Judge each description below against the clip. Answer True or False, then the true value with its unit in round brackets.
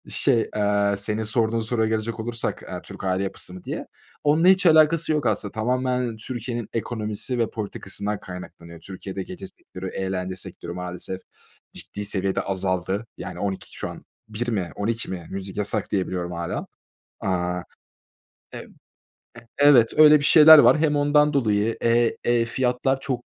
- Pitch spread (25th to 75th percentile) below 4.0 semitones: False (4.6 semitones)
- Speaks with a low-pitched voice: True (110 Hz)